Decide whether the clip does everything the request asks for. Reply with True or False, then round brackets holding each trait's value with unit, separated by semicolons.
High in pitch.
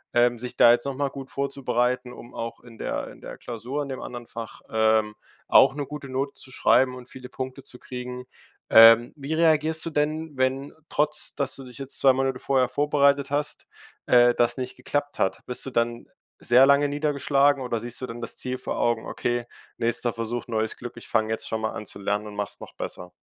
False (125 Hz)